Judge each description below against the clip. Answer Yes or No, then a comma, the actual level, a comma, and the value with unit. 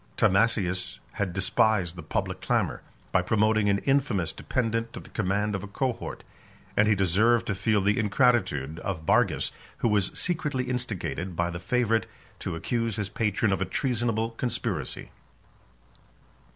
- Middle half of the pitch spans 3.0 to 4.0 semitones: Yes, average, 3.5 semitones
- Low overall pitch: Yes, low, 105 Hz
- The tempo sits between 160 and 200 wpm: No, average, 150 wpm